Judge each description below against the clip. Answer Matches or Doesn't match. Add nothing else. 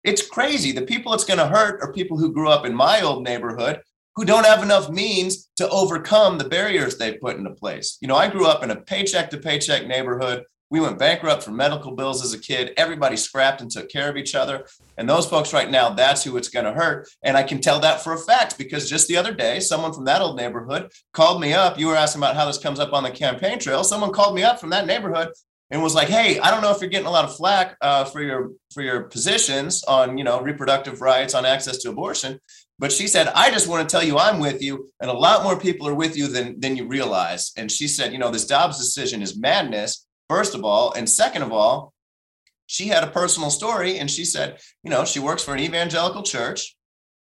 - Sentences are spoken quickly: Matches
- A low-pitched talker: Doesn't match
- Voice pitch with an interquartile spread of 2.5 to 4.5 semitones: Doesn't match